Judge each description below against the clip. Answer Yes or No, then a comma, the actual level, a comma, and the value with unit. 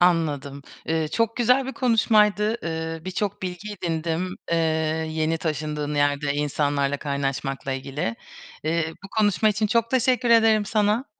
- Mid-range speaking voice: Yes, medium, 165 Hz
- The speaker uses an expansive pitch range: Yes, wide, 6.5 semitones